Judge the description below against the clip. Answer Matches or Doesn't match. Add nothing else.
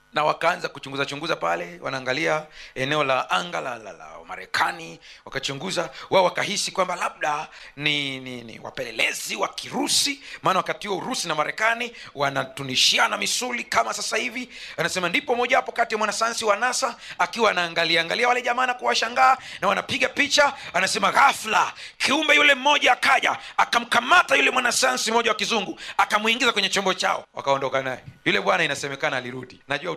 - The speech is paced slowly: Doesn't match